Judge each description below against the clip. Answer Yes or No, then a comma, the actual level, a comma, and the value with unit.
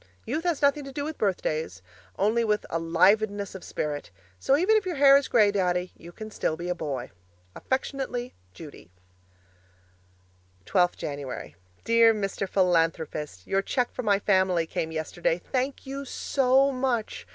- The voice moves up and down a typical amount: No, wide, 7.8 semitones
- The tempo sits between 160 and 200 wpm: No, average, 150 wpm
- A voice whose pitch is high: Yes, high, 200 Hz